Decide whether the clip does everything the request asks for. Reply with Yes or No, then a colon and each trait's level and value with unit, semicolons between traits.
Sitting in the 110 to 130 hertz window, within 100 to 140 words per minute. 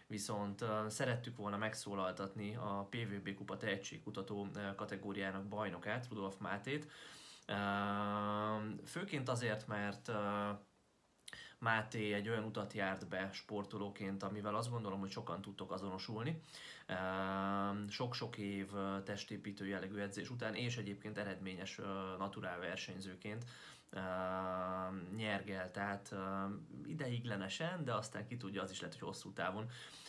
No: low, 100 Hz; slow, 105 wpm